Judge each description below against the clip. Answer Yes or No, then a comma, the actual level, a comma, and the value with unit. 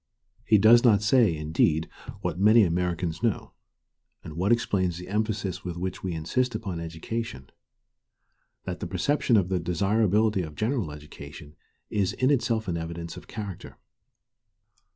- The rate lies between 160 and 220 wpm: No, average, 145 wpm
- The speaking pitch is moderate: No, very low, 95 Hz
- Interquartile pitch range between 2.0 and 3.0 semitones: No, average, 4.8 semitones